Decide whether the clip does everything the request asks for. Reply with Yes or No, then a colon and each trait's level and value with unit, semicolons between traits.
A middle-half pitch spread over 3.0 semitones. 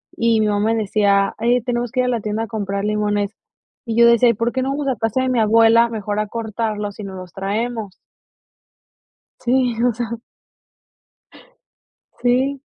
No: narrow, 2.6 semitones